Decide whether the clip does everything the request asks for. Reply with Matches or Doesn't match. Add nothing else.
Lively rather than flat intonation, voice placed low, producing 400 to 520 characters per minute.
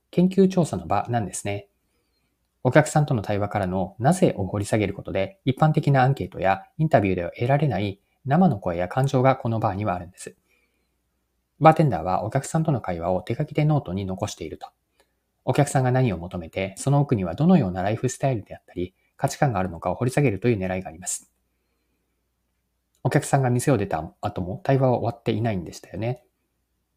Matches